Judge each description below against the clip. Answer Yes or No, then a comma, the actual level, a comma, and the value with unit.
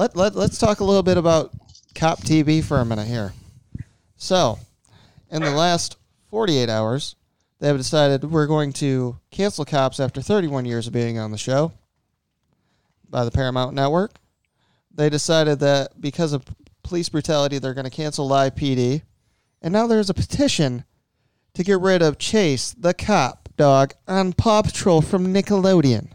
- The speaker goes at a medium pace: Yes, average, 165 wpm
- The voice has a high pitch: No, medium, 145 Hz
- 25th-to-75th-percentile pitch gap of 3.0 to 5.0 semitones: No, wide, 5.5 semitones